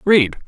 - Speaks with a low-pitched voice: No, medium, 150 Hz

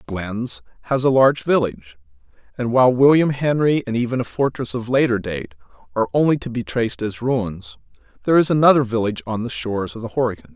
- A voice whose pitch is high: No, low, 120 Hz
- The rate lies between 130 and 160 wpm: No, average, 190 wpm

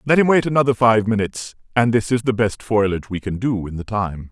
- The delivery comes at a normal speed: No, fast, 250 wpm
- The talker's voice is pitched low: Yes, low, 110 Hz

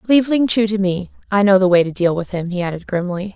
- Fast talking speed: Yes, fast, 285 wpm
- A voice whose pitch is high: Yes, high, 195 Hz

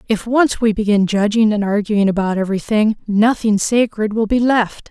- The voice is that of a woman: Yes, female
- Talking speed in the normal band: Yes, average, 170 wpm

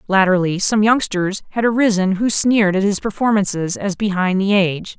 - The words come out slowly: No, average, 170 wpm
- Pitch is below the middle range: No, high, 200 Hz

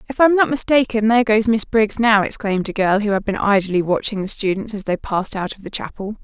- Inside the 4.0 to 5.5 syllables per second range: No, 6.0 syllables/s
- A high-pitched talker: Yes, high, 215 Hz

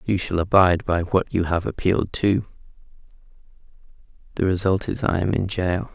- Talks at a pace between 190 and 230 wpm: No, average, 160 wpm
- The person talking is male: Yes, male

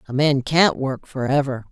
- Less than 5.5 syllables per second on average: Yes, 4.6 syllables/s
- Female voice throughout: Yes, female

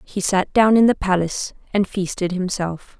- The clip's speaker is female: Yes, female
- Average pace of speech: Yes, average, 180 wpm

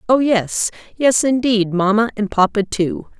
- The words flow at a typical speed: Yes, average, 150 wpm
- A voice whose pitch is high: Yes, high, 220 Hz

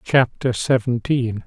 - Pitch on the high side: No, low, 120 Hz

